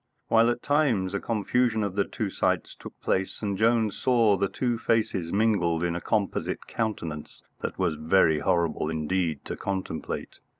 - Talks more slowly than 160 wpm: No, average, 165 wpm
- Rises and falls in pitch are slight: No, average, 4.7 semitones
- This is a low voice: Yes, low, 100 Hz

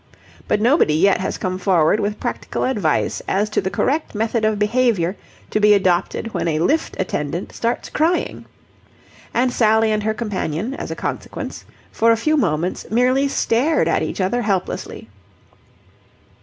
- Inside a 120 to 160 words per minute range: Yes, average, 155 wpm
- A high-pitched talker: Yes, high, 215 Hz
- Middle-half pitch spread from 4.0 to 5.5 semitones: Yes, average, 4.4 semitones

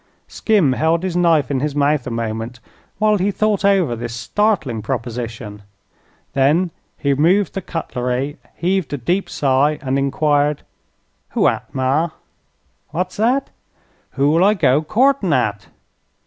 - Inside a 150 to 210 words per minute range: No, slow, 135 wpm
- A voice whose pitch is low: No, medium, 145 Hz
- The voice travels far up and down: Yes, wide, 6.3 semitones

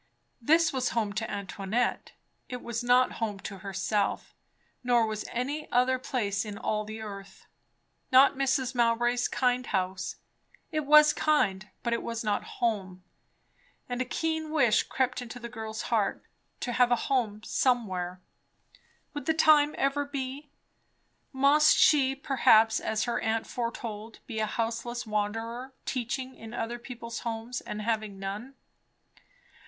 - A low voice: No, high, 235 Hz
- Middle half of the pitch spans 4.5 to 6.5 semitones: No, average, 3.3 semitones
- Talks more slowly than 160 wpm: Yes, average, 145 wpm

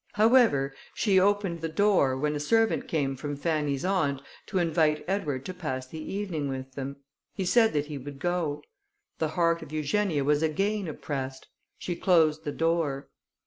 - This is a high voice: No, medium, 155 Hz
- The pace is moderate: Yes, average, 170 wpm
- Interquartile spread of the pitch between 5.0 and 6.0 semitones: No, average, 4.5 semitones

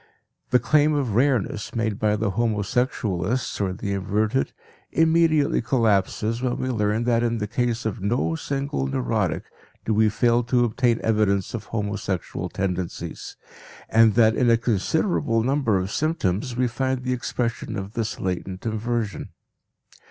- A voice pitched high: No, low, 115 Hz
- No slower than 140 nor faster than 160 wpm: Yes, average, 145 wpm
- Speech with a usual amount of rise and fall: Yes, average, 3.5 semitones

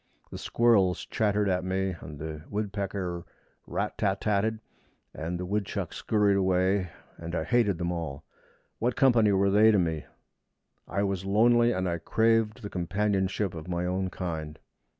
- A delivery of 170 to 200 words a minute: No, average, 160 wpm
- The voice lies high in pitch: No, very low, 95 Hz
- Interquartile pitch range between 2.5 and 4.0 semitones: Yes, average, 3.0 semitones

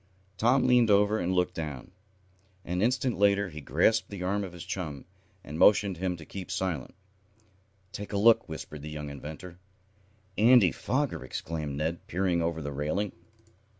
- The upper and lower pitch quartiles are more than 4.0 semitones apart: Yes, average, 4.7 semitones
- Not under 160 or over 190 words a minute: Yes, average, 165 wpm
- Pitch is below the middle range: Yes, very low, 90 Hz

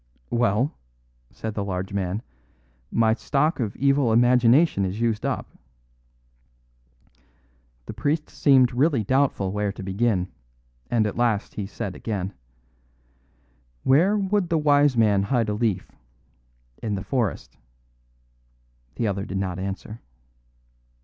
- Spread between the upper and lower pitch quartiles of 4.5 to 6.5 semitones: Yes, average, 5.0 semitones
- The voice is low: Yes, low, 110 Hz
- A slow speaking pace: Yes, slow, 125 wpm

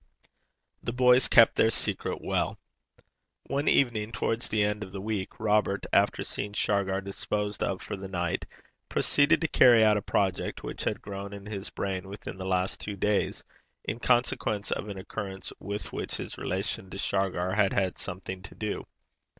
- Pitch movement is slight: Yes, narrow, 2.1 semitones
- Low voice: Yes, low, 100 Hz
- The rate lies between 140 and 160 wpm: No, average, 175 wpm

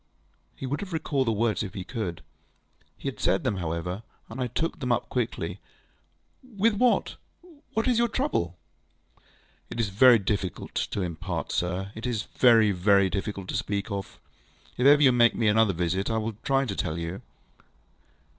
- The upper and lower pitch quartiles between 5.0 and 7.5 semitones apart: Yes, average, 5.3 semitones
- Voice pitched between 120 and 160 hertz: No, low, 110 Hz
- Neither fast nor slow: Yes, average, 180 wpm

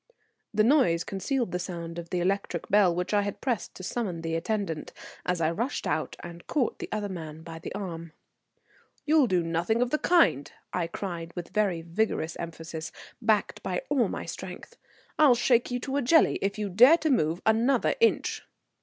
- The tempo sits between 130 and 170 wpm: No, average, 190 wpm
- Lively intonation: Yes, wide, 6.0 semitones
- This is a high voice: Yes, high, 195 Hz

